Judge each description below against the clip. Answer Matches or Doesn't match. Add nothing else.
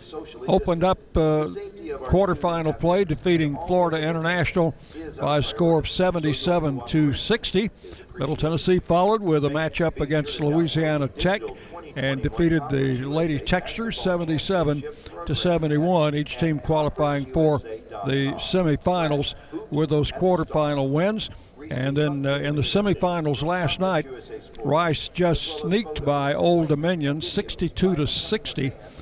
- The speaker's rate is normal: Doesn't match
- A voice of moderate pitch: Matches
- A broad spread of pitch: Doesn't match